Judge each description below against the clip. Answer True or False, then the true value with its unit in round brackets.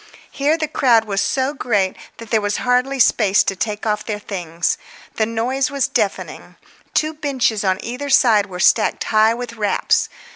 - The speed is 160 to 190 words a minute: True (170 wpm)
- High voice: True (225 Hz)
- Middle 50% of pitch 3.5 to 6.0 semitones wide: True (4.2 semitones)